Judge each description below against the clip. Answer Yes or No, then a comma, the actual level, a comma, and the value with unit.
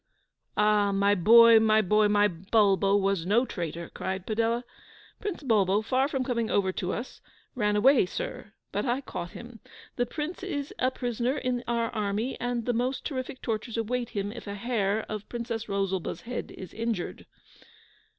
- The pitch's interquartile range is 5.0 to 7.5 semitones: No, average, 3.4 semitones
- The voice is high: Yes, high, 225 Hz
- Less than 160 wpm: No, average, 170 wpm